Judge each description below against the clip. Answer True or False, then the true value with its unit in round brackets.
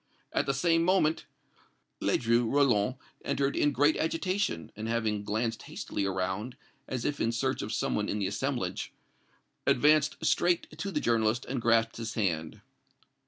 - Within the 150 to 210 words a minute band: True (155 wpm)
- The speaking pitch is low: True (120 Hz)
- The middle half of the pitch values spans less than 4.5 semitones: False (5.2 semitones)